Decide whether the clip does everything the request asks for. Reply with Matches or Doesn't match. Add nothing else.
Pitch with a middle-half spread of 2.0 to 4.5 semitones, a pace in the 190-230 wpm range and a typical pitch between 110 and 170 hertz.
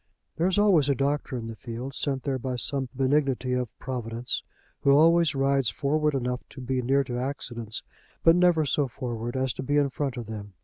Matches